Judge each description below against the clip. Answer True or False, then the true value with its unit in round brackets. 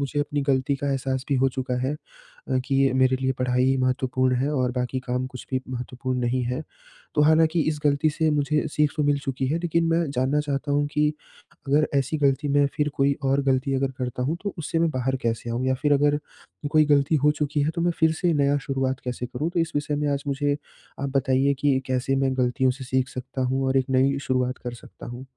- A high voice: False (135 Hz)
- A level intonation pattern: True (2.3 semitones)